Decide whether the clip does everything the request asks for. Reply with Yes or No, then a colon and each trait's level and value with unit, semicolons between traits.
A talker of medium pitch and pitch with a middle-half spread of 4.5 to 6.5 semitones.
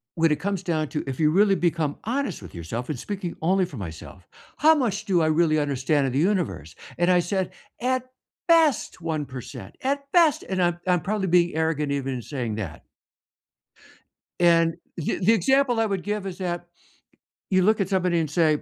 Yes: medium, 175 Hz; average, 4.9 semitones